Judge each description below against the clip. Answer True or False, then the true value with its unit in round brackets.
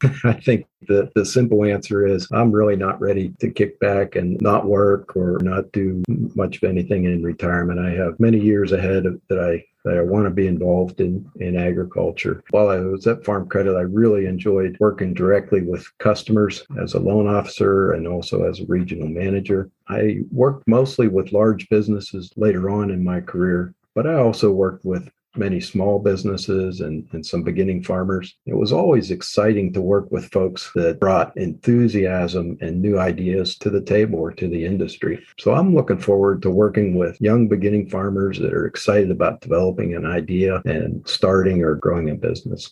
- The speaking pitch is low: True (95 Hz)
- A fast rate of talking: False (185 wpm)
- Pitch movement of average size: False (2.3 semitones)